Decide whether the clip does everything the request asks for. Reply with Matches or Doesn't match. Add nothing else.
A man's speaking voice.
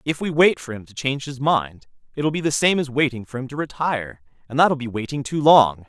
Matches